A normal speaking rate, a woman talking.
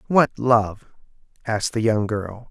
No: average, 145 wpm; male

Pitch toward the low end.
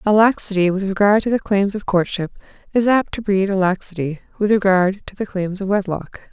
No: high, 195 Hz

